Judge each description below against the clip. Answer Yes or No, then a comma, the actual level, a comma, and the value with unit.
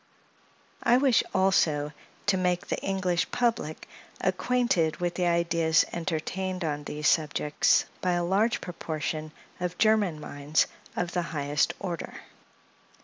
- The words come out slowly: Yes, slow, 125 wpm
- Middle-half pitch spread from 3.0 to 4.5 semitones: Yes, average, 3.4 semitones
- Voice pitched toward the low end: No, medium, 175 Hz